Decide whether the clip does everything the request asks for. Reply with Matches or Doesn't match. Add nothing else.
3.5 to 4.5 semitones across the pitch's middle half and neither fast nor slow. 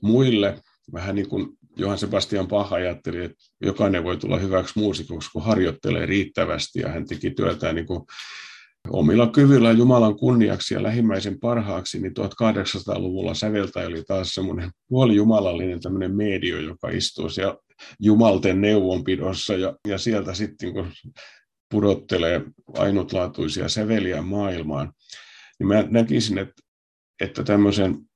Doesn't match